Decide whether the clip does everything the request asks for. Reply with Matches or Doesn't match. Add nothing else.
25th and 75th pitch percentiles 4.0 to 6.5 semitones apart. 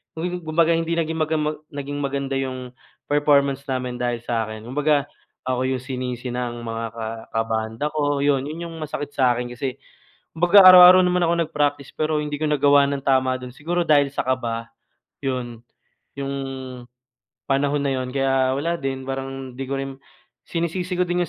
Doesn't match